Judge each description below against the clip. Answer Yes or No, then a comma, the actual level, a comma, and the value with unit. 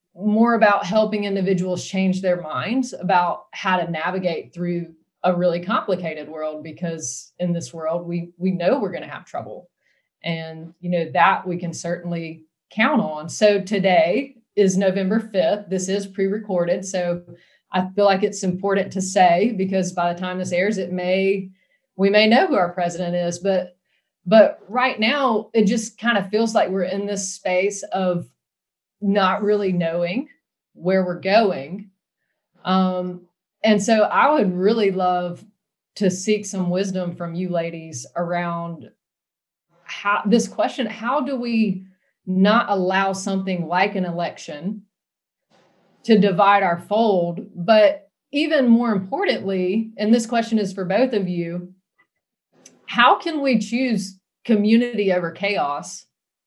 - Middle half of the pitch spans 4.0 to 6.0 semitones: No, average, 3.0 semitones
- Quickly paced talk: No, average, 150 wpm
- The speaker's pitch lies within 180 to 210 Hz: Yes, high, 190 Hz